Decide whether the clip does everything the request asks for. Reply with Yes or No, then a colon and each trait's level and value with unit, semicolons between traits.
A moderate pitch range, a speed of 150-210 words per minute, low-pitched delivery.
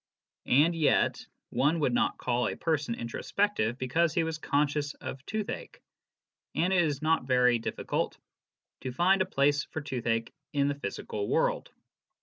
No: average, 4.5 semitones; average, 160 wpm; medium, 145 Hz